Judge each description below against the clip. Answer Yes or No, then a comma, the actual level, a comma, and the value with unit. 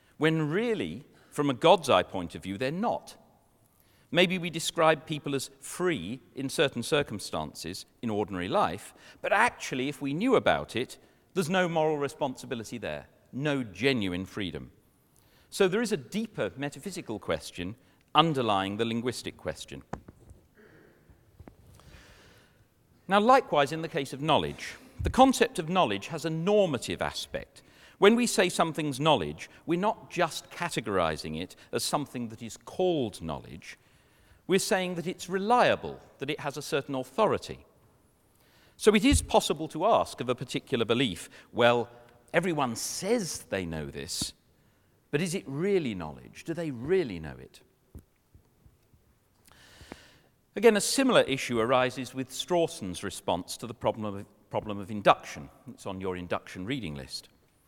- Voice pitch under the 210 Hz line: Yes, medium, 140 Hz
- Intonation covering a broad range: Yes, wide, 8.9 semitones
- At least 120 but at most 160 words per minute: Yes, average, 145 wpm